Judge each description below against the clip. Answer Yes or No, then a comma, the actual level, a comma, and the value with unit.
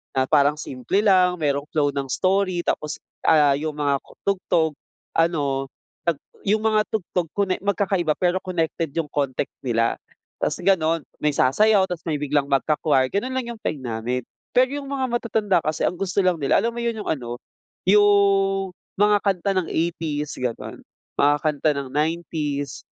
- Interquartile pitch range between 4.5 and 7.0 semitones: Yes, average, 5.3 semitones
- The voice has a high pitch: No, medium, 165 Hz